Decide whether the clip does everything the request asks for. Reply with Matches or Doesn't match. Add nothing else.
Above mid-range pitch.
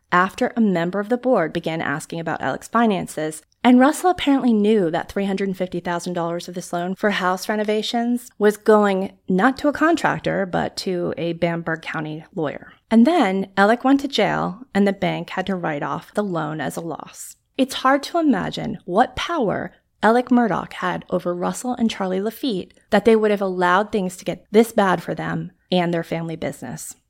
Matches